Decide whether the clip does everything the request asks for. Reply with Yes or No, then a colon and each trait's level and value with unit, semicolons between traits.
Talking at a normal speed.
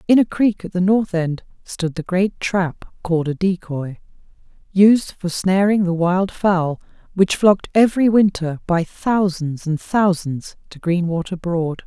Yes: average, 155 wpm